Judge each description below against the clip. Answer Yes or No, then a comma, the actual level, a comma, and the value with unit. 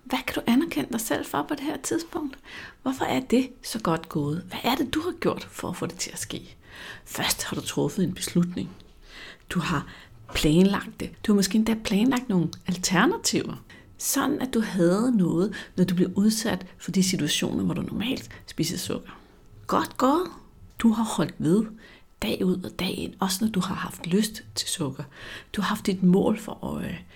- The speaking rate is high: No, average, 200 wpm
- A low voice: No, high, 210 Hz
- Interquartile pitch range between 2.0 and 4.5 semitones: No, wide, 5.4 semitones